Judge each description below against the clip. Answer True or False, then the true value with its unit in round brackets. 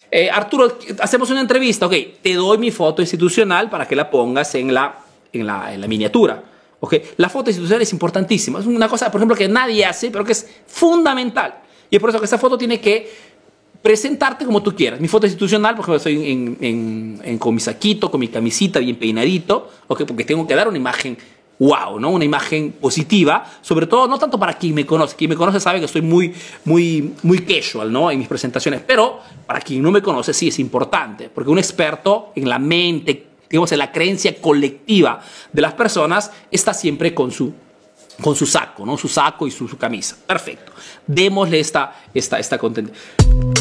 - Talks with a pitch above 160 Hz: True (185 Hz)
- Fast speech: True (200 wpm)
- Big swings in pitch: True (6.0 semitones)